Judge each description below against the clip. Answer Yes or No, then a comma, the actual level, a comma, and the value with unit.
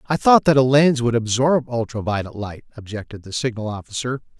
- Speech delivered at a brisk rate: No, average, 190 wpm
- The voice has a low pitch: Yes, low, 120 Hz